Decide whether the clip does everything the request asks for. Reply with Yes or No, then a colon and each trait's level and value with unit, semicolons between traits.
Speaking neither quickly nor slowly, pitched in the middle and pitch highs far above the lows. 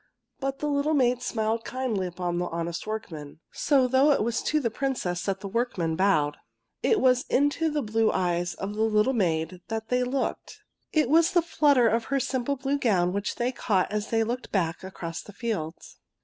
No: average, 195 wpm; high, 225 Hz; wide, 6.2 semitones